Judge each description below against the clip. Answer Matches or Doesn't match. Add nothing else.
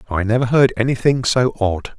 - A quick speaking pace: Doesn't match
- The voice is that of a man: Matches